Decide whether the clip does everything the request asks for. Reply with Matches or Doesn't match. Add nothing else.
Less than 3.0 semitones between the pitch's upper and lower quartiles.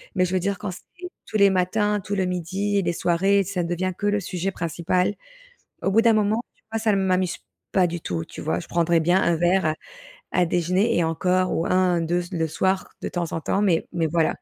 Matches